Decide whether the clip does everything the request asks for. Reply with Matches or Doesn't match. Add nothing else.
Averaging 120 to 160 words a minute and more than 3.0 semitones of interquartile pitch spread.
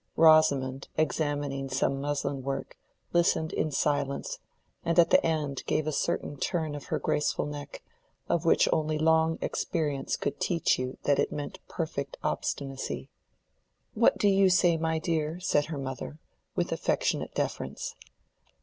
Doesn't match